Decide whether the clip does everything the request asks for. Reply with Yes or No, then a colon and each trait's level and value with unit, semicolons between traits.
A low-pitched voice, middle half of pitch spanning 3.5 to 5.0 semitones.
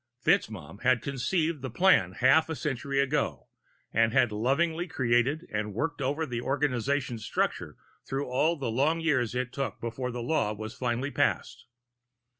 Yes: low, 130 Hz; average, 3.8 semitones